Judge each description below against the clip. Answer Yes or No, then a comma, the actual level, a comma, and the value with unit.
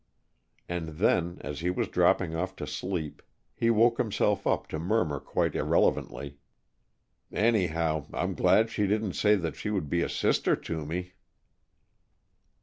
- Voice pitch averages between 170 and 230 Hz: No, very low, 90 Hz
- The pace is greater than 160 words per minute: No, average, 145 wpm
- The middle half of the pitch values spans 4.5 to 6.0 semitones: Yes, average, 4.9 semitones